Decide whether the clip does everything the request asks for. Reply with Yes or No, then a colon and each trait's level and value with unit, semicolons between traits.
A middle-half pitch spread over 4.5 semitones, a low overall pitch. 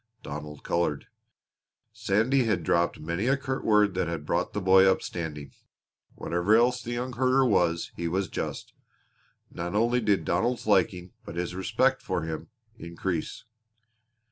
Yes: average, 5.2 semitones; very low, 95 Hz